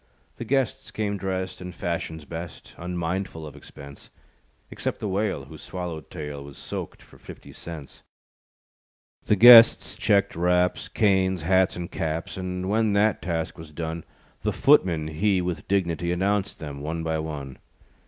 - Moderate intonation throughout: Yes, average, 3.3 semitones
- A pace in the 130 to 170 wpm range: Yes, average, 145 wpm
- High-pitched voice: No, very low, 90 Hz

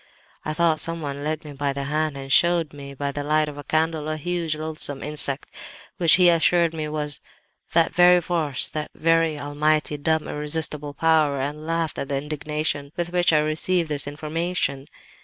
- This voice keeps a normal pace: Yes, average, 180 wpm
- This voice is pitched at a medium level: Yes, medium, 155 Hz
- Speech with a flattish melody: Yes, narrow, 2.1 semitones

